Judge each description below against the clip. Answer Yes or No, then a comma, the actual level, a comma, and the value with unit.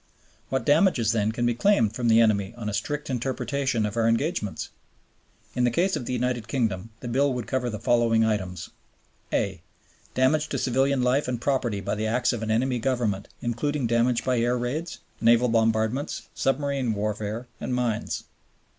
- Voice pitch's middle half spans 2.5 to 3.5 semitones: Yes, average, 2.8 semitones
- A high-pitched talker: No, low, 120 Hz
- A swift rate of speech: No, average, 175 wpm